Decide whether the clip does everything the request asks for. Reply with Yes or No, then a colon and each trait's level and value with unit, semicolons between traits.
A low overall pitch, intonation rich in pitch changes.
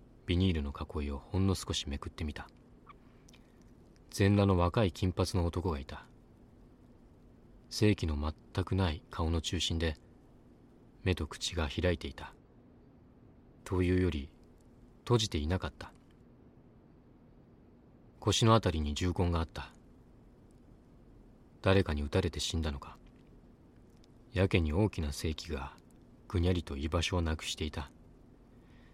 No: very low, 90 Hz; average, 3.4 semitones